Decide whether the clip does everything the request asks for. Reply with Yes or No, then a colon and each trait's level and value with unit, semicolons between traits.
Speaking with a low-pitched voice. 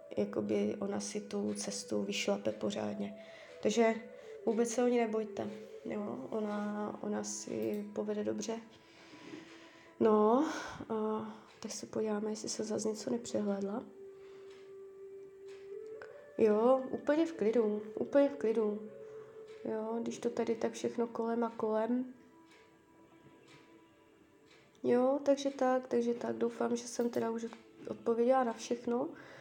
No: high, 230 Hz